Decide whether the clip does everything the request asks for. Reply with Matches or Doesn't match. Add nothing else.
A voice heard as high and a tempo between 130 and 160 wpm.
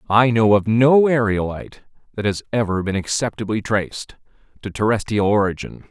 Doesn't match